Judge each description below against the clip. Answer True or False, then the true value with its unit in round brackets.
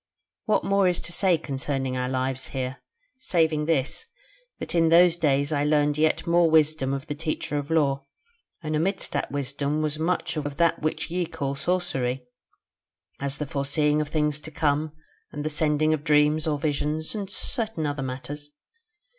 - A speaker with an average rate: True (170 wpm)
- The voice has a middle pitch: True (150 Hz)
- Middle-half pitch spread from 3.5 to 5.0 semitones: False (2.4 semitones)